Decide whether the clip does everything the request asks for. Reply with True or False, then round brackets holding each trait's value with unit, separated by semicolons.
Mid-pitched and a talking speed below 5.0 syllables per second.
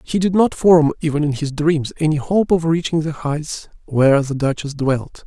True (155 Hz; 4.8 syllables/s)